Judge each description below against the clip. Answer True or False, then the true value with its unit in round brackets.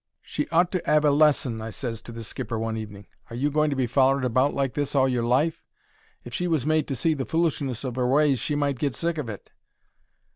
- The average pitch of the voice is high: False (135 Hz)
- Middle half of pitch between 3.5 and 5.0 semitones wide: True (4.1 semitones)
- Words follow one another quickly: True (245 wpm)